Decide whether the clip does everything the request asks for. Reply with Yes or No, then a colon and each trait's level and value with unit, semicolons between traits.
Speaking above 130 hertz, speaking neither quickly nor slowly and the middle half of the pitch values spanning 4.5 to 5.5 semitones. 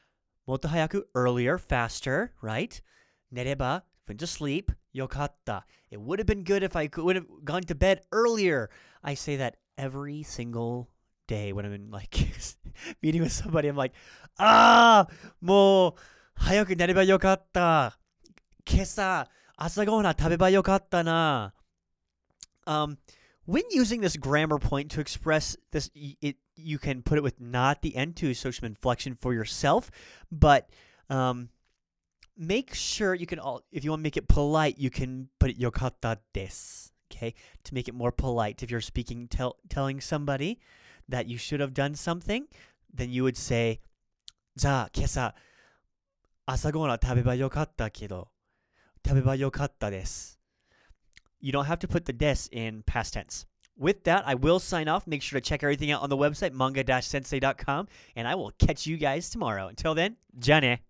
Yes: medium, 140 Hz; average, 155 wpm; average, 5.2 semitones